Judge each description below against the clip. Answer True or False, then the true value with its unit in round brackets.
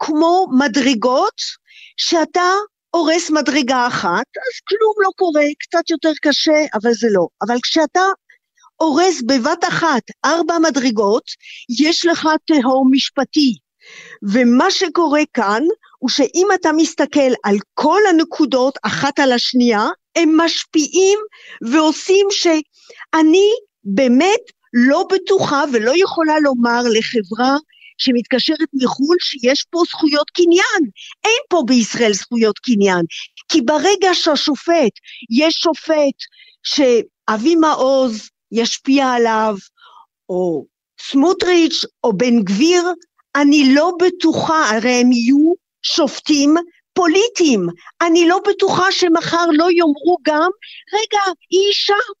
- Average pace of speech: True (110 wpm)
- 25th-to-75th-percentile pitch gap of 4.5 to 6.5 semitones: True (5.6 semitones)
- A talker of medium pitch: False (315 Hz)